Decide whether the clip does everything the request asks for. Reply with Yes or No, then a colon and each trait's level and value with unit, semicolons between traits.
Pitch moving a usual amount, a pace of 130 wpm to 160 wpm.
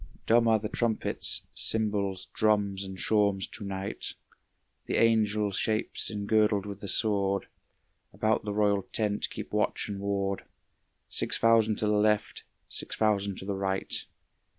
No: narrow, 1.6 semitones; average, 145 wpm